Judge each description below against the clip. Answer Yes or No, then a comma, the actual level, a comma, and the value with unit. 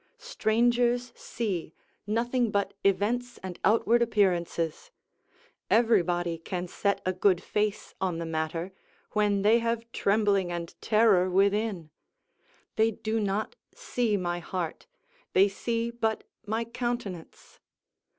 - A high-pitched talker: Yes, high, 205 Hz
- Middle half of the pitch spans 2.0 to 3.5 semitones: No, average, 4.2 semitones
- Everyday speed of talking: No, slow, 115 wpm